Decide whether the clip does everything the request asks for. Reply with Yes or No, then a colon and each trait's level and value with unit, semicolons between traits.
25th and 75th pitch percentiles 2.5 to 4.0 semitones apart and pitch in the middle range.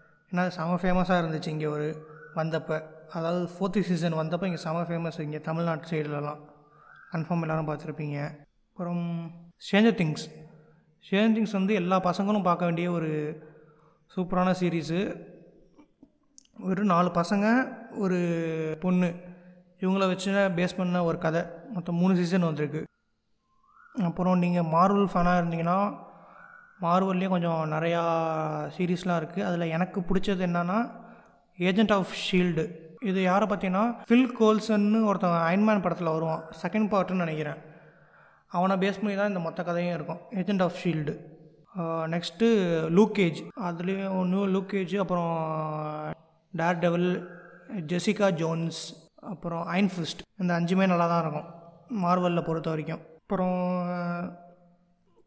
Yes: average, 2.8 semitones; medium, 175 Hz